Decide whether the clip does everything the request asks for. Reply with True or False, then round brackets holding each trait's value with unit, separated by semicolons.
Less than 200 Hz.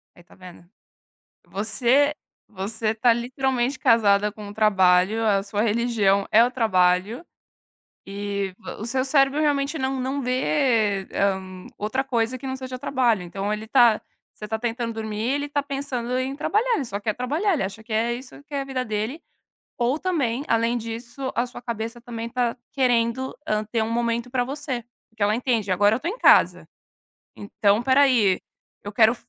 False (235 Hz)